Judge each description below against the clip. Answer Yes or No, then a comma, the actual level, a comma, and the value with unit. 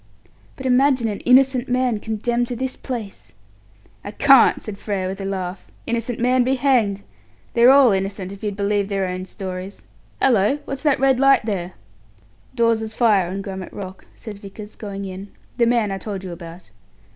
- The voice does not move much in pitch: No, average, 4.2 semitones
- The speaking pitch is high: Yes, high, 210 Hz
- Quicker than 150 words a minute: Yes, average, 175 wpm